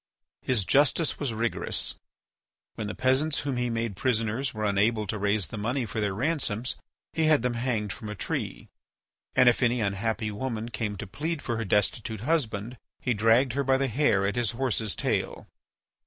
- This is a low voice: Yes, low, 115 Hz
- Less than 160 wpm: No, average, 185 wpm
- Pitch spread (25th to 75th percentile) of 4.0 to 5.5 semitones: No, average, 3.6 semitones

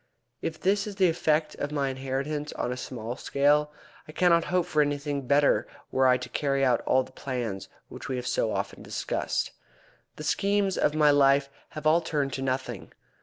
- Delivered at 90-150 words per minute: No, average, 185 wpm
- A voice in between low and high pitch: Yes, medium, 145 Hz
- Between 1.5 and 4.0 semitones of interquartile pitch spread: Yes, average, 2.7 semitones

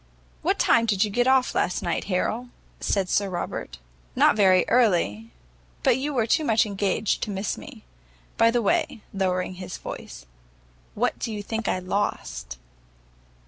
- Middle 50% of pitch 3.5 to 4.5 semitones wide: Yes, average, 3.9 semitones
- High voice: Yes, high, 200 Hz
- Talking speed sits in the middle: Yes, average, 160 wpm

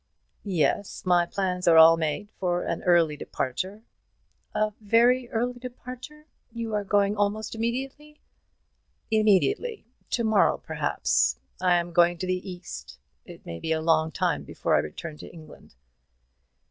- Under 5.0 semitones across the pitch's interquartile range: No, wide, 5.5 semitones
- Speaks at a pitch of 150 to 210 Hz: Yes, high, 190 Hz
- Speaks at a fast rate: No, average, 145 wpm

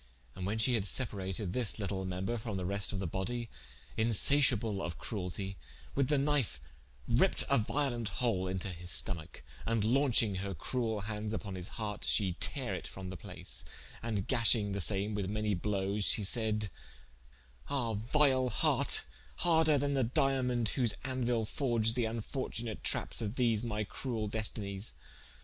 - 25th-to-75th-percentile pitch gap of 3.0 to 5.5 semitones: Yes, average, 3.6 semitones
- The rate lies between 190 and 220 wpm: No, average, 160 wpm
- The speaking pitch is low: Yes, low, 110 Hz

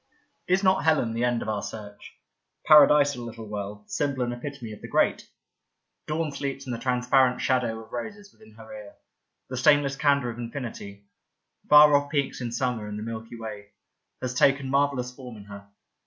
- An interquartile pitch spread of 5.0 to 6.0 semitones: No, average, 4.0 semitones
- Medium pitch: No, low, 125 Hz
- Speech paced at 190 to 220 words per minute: Yes, average, 195 wpm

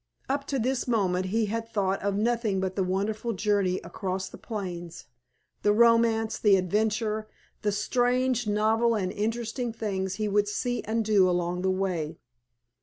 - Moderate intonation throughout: Yes, average, 3.2 semitones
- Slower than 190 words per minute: Yes, average, 160 wpm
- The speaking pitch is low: No, high, 210 Hz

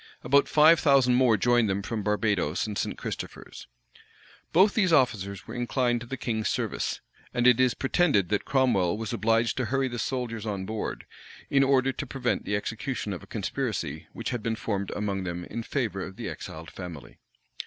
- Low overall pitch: Yes, low, 115 Hz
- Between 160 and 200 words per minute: Yes, average, 185 wpm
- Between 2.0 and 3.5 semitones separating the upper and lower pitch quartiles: No, average, 4.2 semitones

